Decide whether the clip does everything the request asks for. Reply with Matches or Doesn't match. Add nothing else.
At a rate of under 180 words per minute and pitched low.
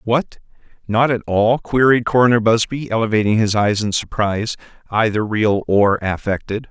Matches